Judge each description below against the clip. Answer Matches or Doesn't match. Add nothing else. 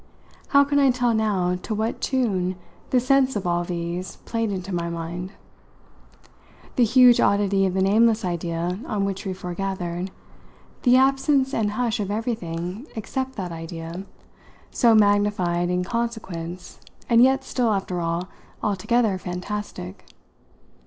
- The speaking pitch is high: Matches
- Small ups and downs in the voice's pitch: Doesn't match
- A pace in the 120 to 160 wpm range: Matches